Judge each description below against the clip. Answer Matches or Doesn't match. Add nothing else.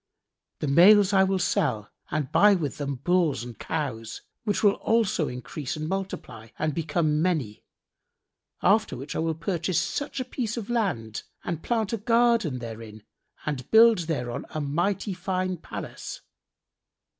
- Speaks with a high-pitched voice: Doesn't match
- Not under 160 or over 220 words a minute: Doesn't match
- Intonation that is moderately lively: Doesn't match